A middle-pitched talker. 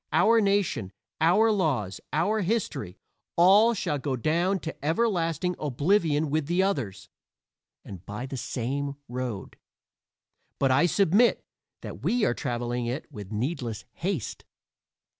Yes: medium, 155 Hz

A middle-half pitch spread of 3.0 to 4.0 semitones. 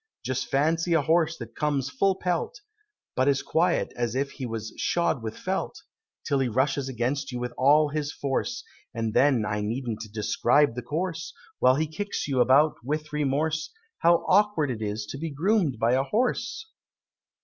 No: average, 4.6 semitones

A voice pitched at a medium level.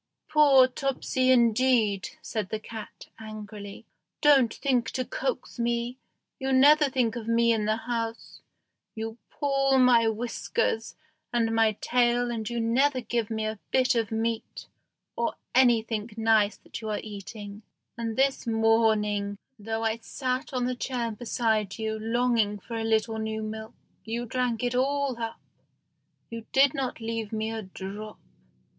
No: high, 230 Hz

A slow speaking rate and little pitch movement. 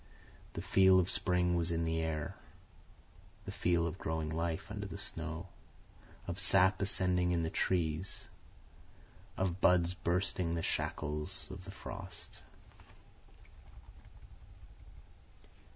Yes: slow, 115 wpm; narrow, 2.3 semitones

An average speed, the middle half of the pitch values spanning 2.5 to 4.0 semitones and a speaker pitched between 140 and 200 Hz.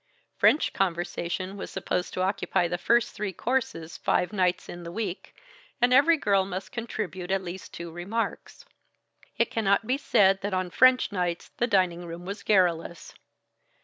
Yes: average, 160 wpm; average, 3.4 semitones; high, 190 Hz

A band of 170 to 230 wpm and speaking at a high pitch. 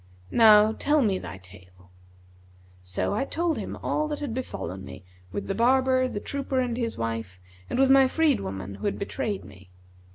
Yes: average, 185 wpm; high, 215 Hz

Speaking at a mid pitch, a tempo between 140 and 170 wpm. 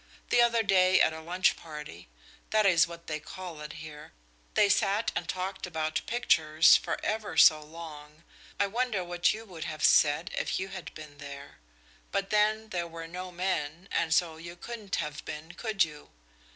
No: medium, 175 Hz; average, 180 wpm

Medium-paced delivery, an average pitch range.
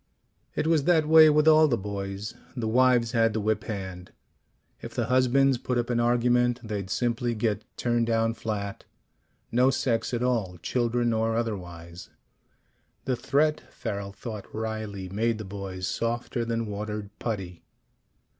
Yes: average, 150 wpm; average, 3.2 semitones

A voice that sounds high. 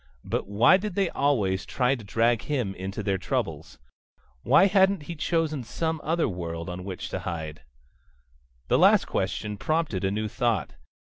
No: low, 115 Hz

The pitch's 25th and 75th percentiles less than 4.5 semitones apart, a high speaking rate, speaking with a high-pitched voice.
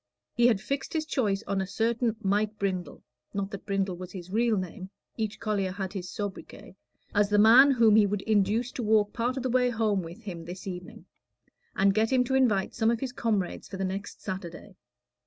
Yes: average, 3.2 semitones; fast, 210 wpm; high, 205 Hz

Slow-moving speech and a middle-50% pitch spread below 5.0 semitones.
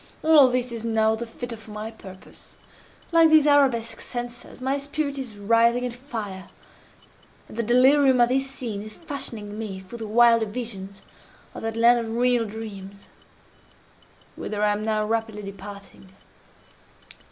No: average, 150 wpm; average, 2.9 semitones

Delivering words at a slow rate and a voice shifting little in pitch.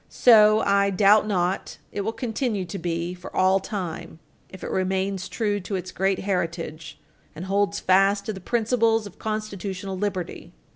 No: average, 160 wpm; narrow, 2.3 semitones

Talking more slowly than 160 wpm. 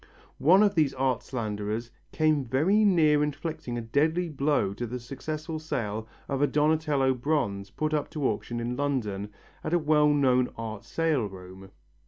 No: average, 165 wpm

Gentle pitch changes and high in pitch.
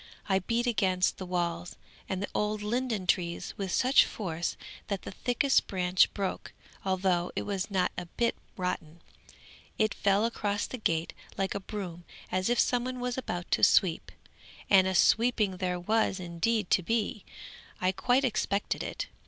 No: average, 3.7 semitones; high, 195 Hz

